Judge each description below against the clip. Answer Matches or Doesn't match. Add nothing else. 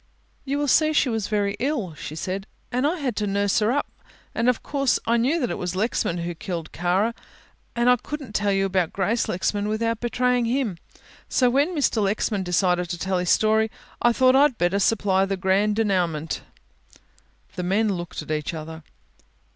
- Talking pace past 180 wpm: Matches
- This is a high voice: Matches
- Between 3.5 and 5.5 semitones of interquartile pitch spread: Matches